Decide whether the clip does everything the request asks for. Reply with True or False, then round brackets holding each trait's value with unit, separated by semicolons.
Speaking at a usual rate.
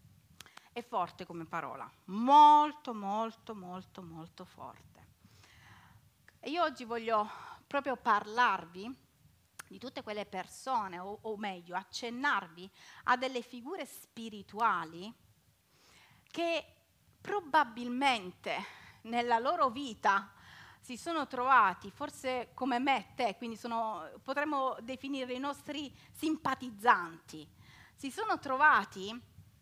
False (100 wpm)